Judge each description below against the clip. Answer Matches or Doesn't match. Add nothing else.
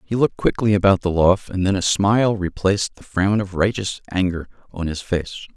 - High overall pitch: Doesn't match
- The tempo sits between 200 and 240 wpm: Matches